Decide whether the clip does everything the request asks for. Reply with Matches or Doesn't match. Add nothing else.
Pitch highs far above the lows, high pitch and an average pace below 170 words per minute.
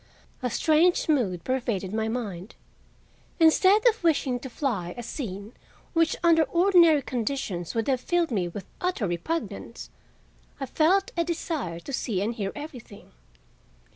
Matches